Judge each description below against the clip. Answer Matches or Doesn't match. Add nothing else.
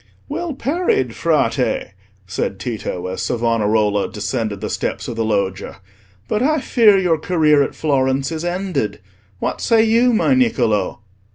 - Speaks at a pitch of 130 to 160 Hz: Matches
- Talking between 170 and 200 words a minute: Doesn't match